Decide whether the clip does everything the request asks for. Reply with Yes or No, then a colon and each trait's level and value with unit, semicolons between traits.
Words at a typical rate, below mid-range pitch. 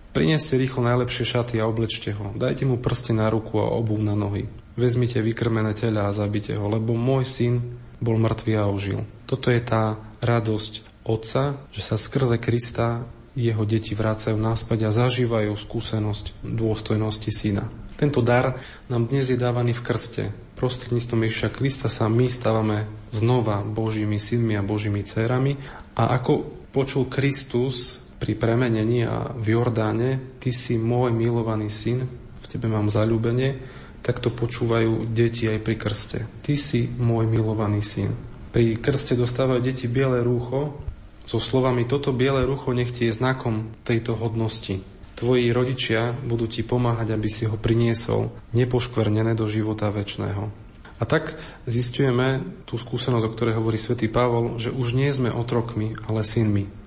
Yes: average, 150 wpm; low, 115 Hz